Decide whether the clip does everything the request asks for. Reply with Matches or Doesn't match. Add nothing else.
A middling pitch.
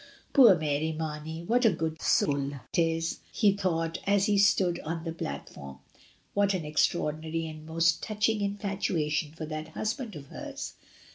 Matches